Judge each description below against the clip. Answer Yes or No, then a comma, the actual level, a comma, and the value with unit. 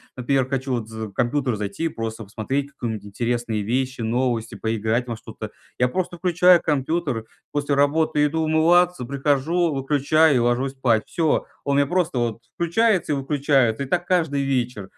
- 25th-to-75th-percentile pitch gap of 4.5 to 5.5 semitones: Yes, average, 5.0 semitones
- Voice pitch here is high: No, low, 135 Hz